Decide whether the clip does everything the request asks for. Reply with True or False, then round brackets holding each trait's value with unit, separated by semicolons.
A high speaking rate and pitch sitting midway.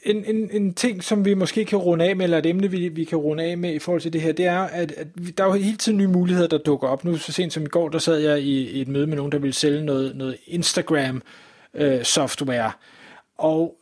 True (270 wpm; 165 Hz)